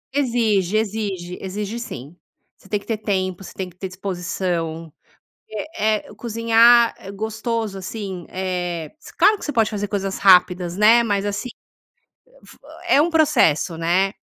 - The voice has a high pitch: Yes, high, 200 Hz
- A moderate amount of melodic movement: Yes, average, 3.6 semitones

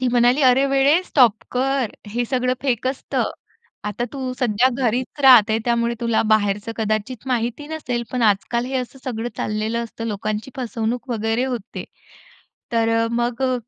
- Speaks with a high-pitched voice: Yes, high, 240 Hz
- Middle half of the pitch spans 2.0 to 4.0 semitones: Yes, narrow, 2.5 semitones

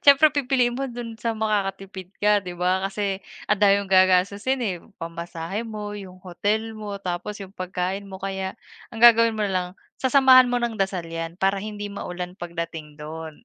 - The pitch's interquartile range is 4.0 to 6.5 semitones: No, average, 3.5 semitones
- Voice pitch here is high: Yes, high, 195 Hz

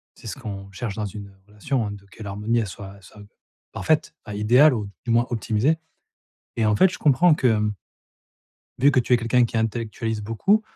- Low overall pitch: Yes, low, 110 Hz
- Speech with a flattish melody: No, average, 3.2 semitones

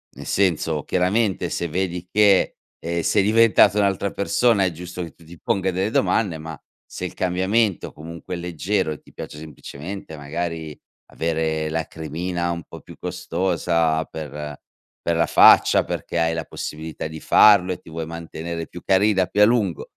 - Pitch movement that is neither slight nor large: Yes, average, 3.0 semitones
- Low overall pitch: Yes, very low, 85 Hz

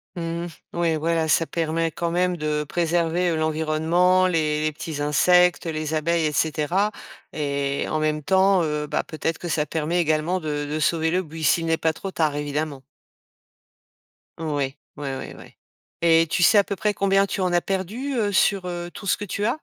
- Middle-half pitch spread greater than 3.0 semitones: No, average, 2.7 semitones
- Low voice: No, medium, 165 Hz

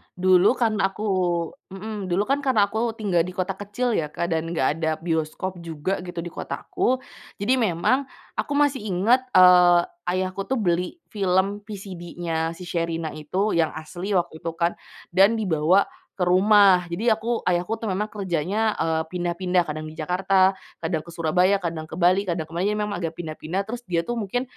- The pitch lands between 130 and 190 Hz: Yes, medium, 185 Hz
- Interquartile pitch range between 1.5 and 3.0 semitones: No, average, 3.5 semitones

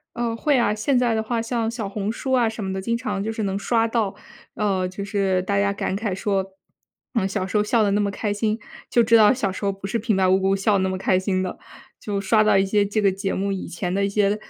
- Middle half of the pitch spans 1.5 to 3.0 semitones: Yes, narrow, 2.5 semitones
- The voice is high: Yes, high, 205 Hz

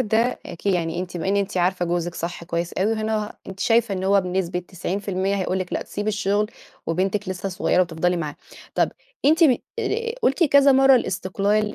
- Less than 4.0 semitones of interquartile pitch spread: Yes, average, 3.2 semitones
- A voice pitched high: Yes, high, 195 Hz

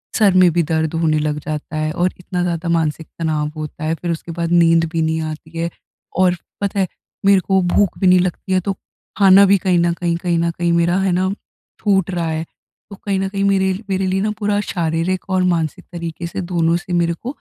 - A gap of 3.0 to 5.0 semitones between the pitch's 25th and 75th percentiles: No, narrow, 2.4 semitones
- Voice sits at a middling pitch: Yes, medium, 175 Hz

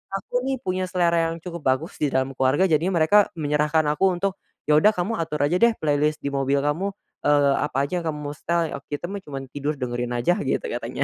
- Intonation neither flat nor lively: Yes, average, 3.8 semitones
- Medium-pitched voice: Yes, medium, 150 Hz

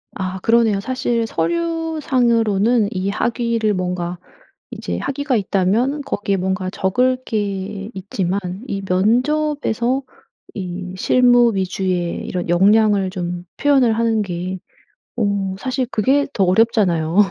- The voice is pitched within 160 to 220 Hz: Yes, high, 205 Hz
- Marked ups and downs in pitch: No, average, 4.5 semitones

